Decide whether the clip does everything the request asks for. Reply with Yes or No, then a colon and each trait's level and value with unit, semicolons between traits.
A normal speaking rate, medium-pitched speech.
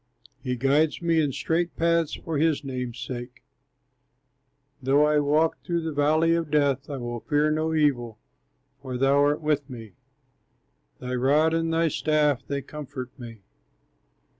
Yes: average, 150 wpm; medium, 145 Hz